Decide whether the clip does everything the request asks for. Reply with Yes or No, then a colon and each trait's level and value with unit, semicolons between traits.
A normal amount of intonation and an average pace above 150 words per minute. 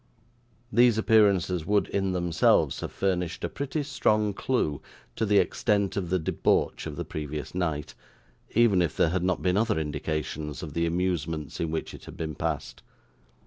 Yes: average, 4.5 semitones; average, 170 wpm